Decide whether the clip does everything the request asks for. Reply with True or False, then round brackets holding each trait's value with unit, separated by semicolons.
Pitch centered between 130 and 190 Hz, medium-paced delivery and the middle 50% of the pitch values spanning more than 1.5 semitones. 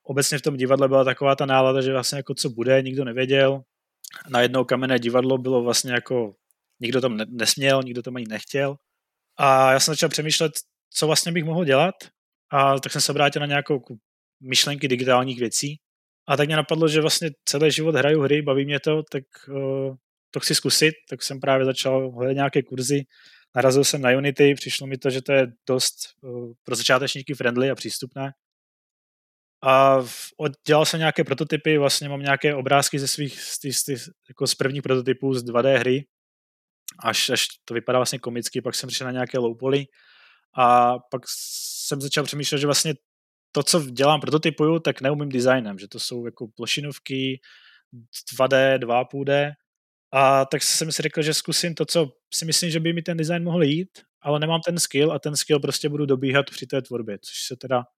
False (135 Hz; 185 wpm; 2.5 semitones)